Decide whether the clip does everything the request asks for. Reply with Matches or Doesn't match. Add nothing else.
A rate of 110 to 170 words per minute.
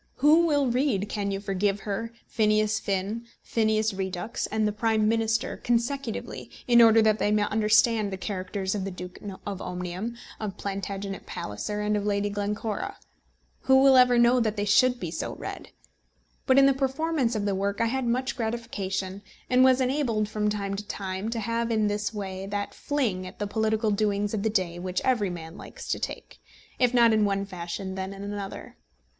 Doesn't match